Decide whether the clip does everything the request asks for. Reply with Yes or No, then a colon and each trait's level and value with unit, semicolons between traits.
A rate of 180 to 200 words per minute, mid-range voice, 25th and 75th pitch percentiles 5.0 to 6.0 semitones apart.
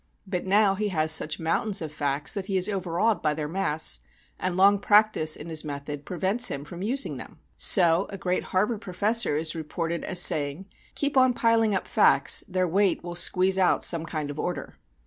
No: average, 195 wpm; medium, 180 Hz; average, 4.2 semitones